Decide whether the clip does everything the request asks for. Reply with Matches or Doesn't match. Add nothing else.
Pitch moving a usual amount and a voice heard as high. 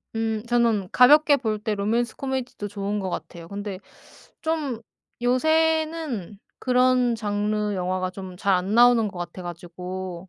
Matches